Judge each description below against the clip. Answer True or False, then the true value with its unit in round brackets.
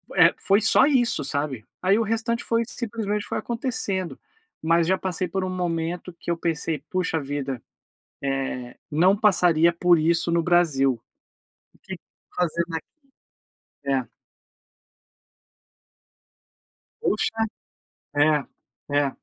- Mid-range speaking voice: True (170 Hz)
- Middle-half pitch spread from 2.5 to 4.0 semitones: False (4.7 semitones)